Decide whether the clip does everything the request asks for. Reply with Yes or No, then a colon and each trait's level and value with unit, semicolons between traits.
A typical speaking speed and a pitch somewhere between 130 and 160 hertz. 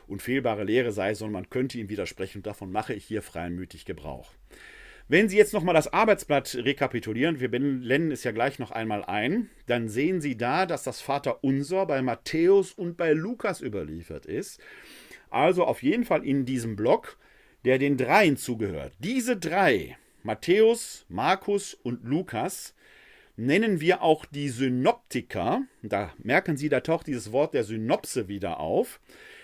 Yes: average, 155 wpm; medium, 140 Hz